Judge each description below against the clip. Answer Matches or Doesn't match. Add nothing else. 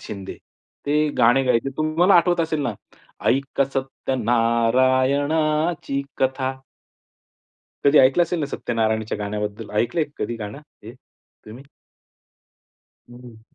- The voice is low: Matches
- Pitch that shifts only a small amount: Doesn't match